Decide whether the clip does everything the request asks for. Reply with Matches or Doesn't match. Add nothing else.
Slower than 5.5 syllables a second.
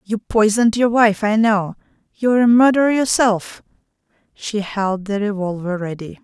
Matches